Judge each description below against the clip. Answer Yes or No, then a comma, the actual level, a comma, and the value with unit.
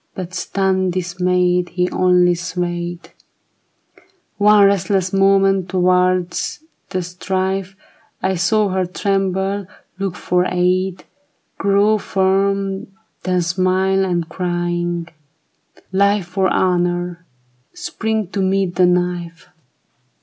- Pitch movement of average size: No, narrow, 1.5 semitones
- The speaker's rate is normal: No, slow, 105 wpm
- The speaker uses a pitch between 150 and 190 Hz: Yes, medium, 185 Hz